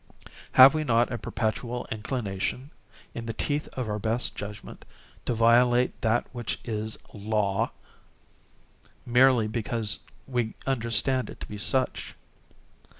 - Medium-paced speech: No, slow, 125 wpm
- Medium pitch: No, low, 115 Hz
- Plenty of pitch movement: No, narrow, 2.5 semitones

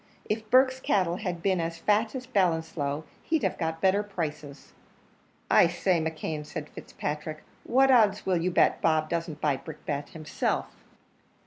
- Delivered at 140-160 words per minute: Yes, average, 150 wpm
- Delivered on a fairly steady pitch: No, average, 4.8 semitones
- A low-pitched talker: No, medium, 170 Hz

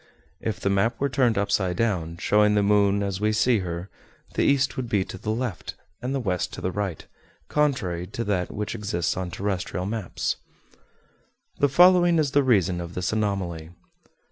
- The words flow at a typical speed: Yes, average, 180 wpm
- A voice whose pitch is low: Yes, low, 100 Hz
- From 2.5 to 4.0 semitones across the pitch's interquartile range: No, average, 4.5 semitones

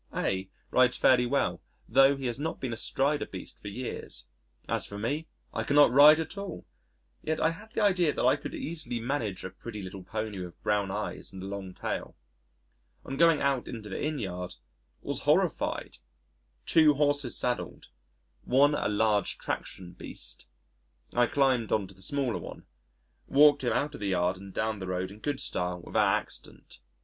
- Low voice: Yes, low, 120 Hz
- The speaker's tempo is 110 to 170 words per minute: No, average, 180 wpm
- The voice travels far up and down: Yes, wide, 6.6 semitones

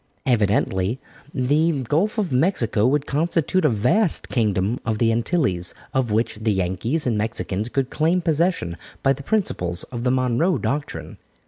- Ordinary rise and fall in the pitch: No, wide, 6.4 semitones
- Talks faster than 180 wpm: No, average, 150 wpm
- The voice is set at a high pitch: No, low, 125 Hz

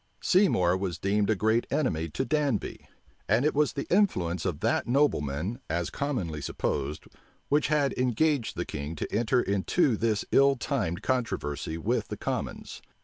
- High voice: No, low, 110 Hz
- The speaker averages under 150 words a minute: No, average, 155 wpm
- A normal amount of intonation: No, wide, 8.3 semitones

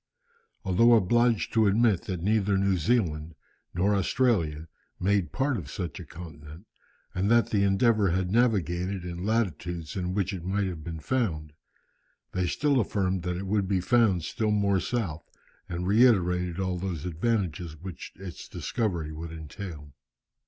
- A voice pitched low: Yes, very low, 95 Hz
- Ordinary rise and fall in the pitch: Yes, average, 3.5 semitones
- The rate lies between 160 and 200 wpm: No, average, 150 wpm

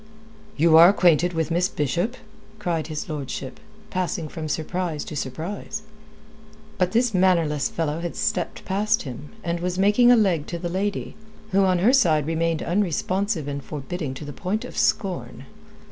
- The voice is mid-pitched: Yes, medium, 175 Hz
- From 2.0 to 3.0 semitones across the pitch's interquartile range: No, average, 3.8 semitones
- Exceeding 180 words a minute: No, average, 160 wpm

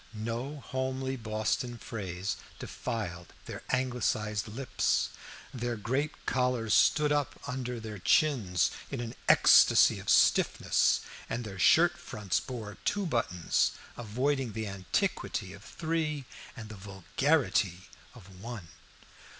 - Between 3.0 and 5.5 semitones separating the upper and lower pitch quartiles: Yes, average, 4.5 semitones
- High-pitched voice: No, low, 115 Hz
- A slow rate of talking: Yes, slow, 120 wpm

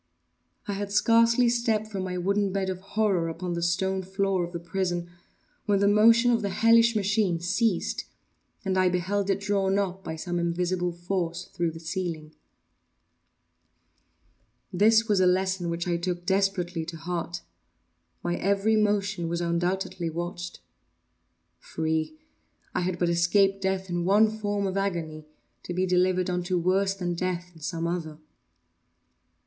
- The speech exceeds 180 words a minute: No, average, 150 wpm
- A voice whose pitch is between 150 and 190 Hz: Yes, medium, 185 Hz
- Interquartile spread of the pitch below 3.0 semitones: Yes, narrow, 2.5 semitones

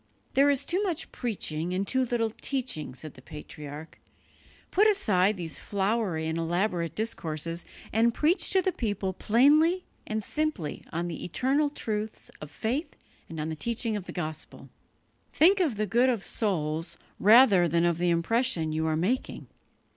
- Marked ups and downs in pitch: Yes, wide, 7.6 semitones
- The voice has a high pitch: Yes, high, 205 Hz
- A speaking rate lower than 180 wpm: Yes, average, 160 wpm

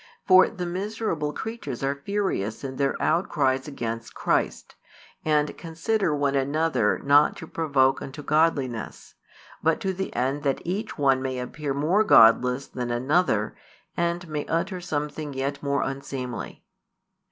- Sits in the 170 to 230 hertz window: No, medium, 145 Hz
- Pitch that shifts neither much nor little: Yes, average, 4.0 semitones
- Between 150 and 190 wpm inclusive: No, average, 140 wpm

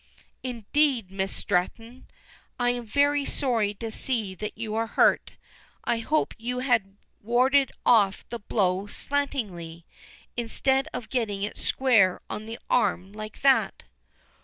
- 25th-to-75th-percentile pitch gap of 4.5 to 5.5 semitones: No, average, 4.0 semitones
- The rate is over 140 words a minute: No, slow, 135 wpm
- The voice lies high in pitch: Yes, high, 225 Hz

